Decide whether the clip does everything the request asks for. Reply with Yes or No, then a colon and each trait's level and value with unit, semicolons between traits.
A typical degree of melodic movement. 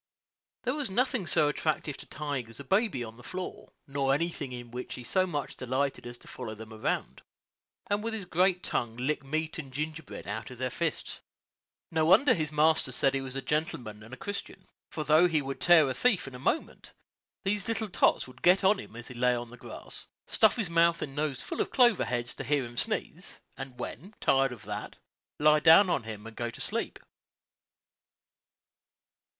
No: wide, 5.8 semitones